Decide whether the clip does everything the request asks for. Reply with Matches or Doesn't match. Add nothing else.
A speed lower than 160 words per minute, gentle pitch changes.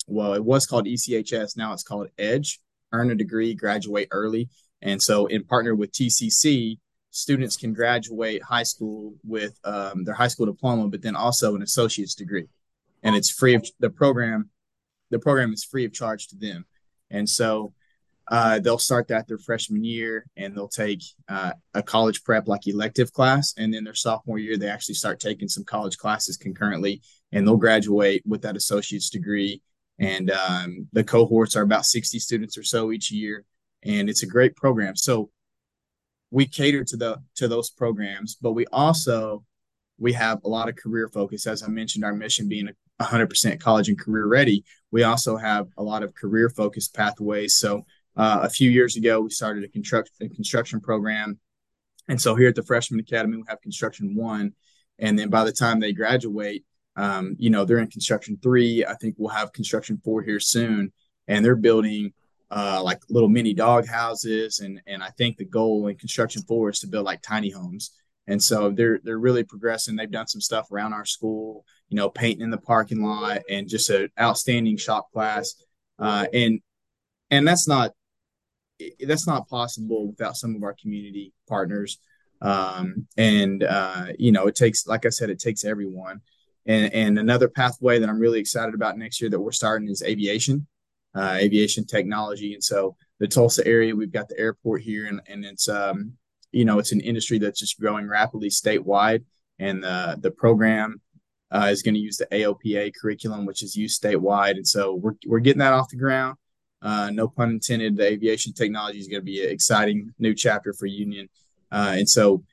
Doesn't match